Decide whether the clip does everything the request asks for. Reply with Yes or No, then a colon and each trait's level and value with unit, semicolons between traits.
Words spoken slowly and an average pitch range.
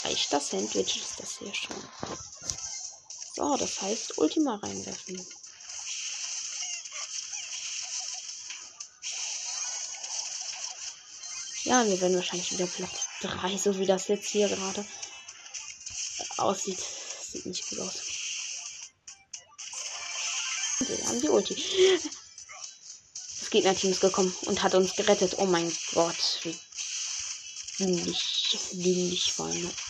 No: slow, 95 wpm; narrow, 2.2 semitones